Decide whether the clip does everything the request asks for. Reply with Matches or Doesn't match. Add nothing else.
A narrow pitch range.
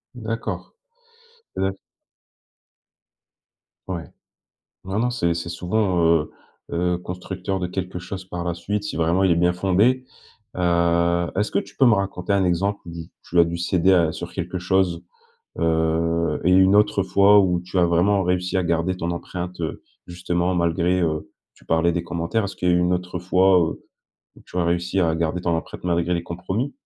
Matches